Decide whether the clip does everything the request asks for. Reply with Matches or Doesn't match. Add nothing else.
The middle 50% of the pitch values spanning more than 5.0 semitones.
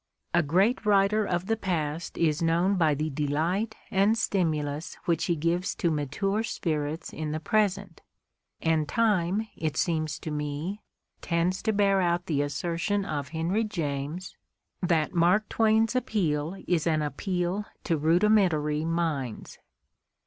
Doesn't match